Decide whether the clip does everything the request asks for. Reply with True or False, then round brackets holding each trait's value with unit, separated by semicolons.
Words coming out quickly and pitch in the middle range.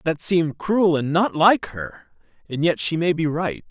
True (210 wpm; 155 Hz)